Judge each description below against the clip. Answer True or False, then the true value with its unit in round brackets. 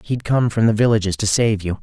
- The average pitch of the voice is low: True (110 Hz)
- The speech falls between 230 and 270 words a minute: True (265 wpm)